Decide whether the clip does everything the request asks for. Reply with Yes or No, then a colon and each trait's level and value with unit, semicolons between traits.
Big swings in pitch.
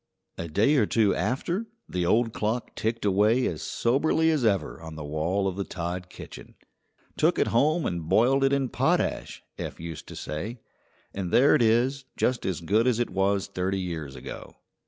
Yes: wide, 5.8 semitones